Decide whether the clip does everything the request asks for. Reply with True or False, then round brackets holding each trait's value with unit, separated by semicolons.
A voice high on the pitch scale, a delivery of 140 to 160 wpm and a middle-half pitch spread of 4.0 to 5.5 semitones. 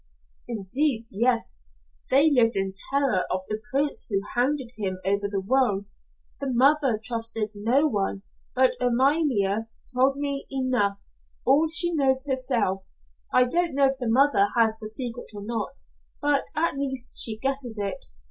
True (250 Hz; 150 wpm; 4.4 semitones)